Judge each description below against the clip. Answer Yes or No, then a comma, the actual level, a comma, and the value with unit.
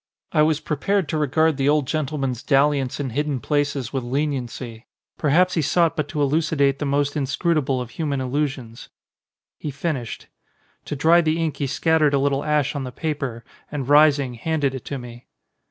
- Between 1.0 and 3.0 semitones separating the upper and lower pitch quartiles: Yes, narrow, 2.5 semitones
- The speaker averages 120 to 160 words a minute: No, average, 185 wpm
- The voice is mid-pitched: Yes, medium, 145 Hz